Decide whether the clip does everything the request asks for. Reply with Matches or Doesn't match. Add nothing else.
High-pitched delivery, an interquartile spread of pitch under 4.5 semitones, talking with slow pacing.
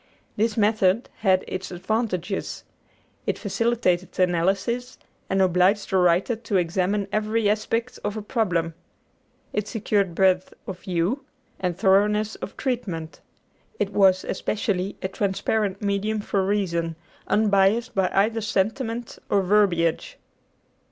Matches